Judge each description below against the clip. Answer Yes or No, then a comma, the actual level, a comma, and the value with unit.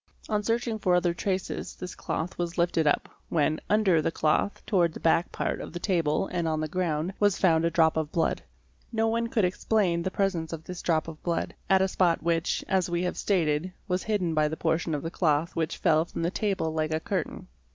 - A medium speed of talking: No, fast, 225 wpm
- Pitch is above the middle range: No, medium, 170 Hz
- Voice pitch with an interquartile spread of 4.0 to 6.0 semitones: No, average, 2.9 semitones